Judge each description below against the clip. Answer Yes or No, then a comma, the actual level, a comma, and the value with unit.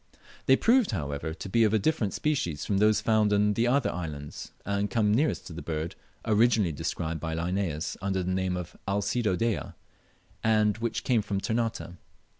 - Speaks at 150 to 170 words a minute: No, average, 180 wpm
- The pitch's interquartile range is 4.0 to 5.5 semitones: Yes, average, 4.5 semitones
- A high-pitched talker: No, low, 100 Hz